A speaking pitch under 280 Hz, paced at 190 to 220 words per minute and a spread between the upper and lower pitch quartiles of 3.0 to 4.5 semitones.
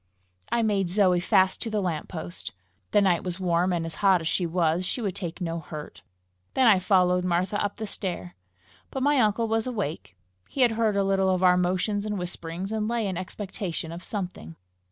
Yes: medium, 185 Hz; average, 200 wpm; average, 3.3 semitones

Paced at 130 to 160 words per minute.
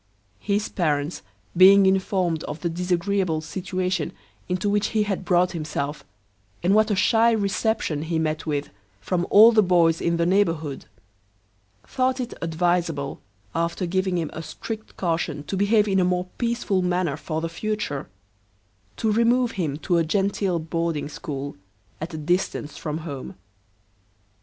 Yes: average, 150 wpm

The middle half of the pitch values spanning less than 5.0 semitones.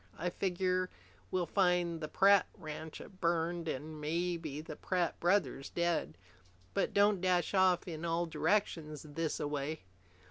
Yes: average, 2.7 semitones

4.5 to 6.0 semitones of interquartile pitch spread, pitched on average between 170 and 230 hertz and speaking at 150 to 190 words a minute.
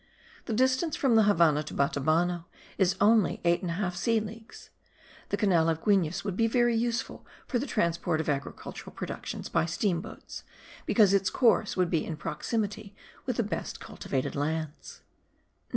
Yes: average, 5.3 semitones; high, 190 Hz; average, 170 wpm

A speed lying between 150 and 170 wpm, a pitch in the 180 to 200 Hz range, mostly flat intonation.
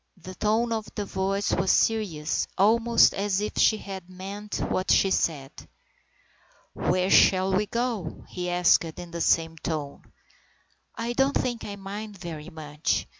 No: average, 155 wpm; high, 190 Hz; average, 3.6 semitones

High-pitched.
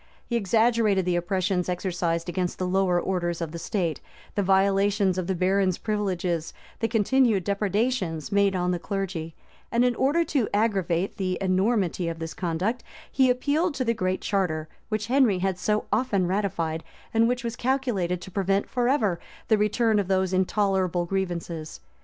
Yes: high, 195 Hz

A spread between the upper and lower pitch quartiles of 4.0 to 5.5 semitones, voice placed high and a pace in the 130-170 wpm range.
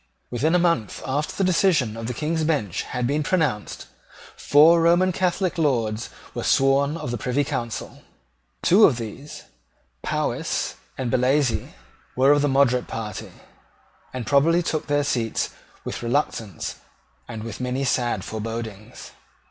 No: average, 4.9 semitones; low, 135 Hz; average, 140 wpm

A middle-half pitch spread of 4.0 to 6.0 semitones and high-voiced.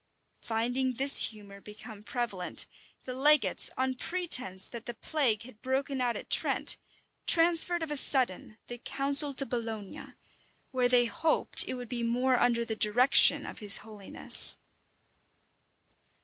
No: average, 3.5 semitones; high, 245 Hz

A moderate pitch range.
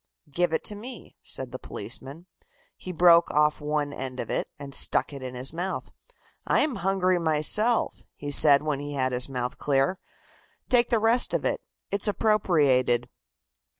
No: wide, 5.9 semitones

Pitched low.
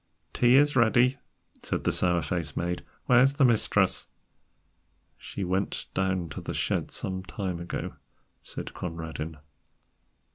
Yes: very low, 95 Hz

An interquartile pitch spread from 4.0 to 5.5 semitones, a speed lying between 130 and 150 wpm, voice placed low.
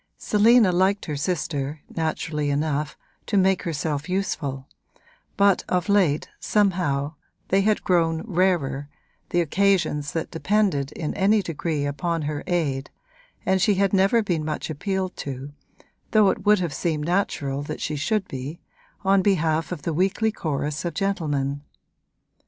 No: average, 4.8 semitones; average, 140 wpm; medium, 170 Hz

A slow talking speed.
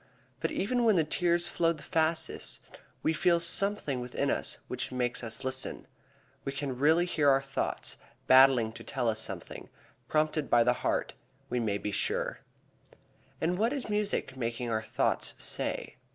No: average, 165 wpm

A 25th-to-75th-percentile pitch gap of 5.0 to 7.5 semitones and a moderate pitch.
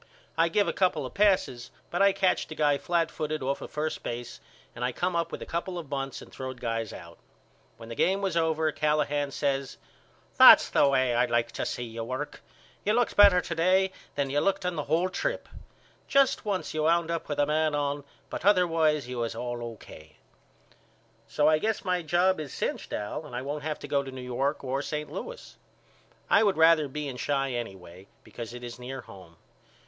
Yes: average, 5.3 semitones; medium, 150 Hz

